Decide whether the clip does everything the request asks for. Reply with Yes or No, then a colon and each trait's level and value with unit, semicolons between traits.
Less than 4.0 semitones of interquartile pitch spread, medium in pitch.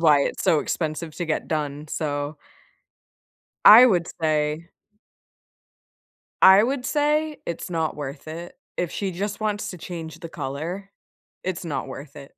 No: average, 4.4 semitones; medium, 165 Hz